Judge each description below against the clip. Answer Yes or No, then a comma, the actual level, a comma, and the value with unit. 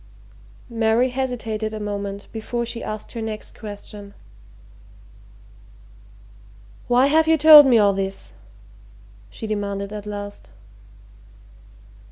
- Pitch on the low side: No, high, 215 Hz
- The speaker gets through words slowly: Yes, slow, 105 wpm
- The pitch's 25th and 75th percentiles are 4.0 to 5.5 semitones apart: No, average, 3.1 semitones